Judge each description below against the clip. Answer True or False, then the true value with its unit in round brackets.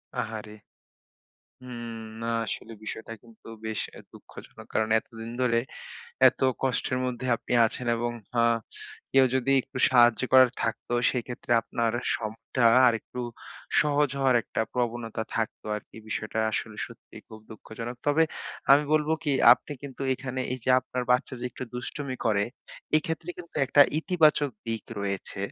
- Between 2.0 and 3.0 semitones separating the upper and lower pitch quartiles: True (2.7 semitones)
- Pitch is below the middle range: True (120 Hz)